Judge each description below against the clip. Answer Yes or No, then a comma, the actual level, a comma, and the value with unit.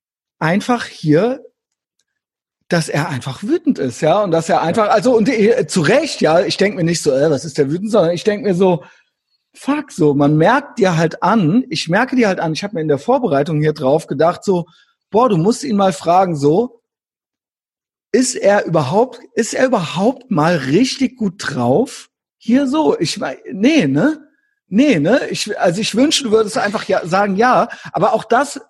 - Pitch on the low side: No, high, 200 Hz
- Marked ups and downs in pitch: Yes, wide, 7.0 semitones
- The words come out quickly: Yes, fast, 195 wpm